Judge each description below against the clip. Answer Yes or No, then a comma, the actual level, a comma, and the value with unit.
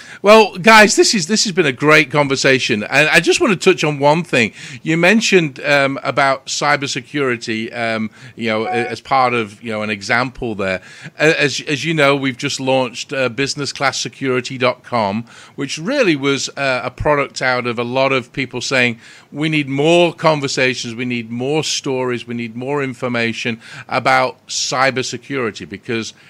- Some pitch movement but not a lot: Yes, average, 3.2 semitones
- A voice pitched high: No, low, 135 Hz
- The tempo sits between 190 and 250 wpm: No, average, 165 wpm